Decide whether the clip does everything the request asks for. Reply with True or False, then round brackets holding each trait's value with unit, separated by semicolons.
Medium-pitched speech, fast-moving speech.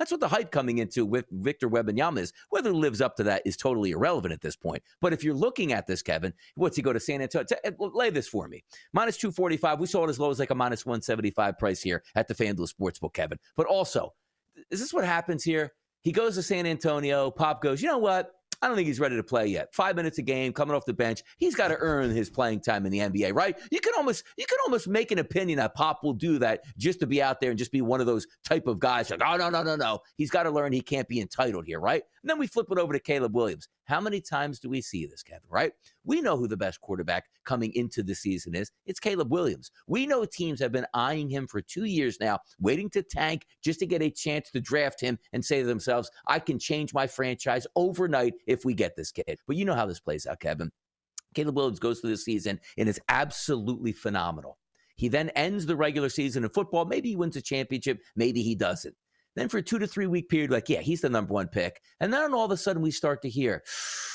True (145 Hz; 260 wpm)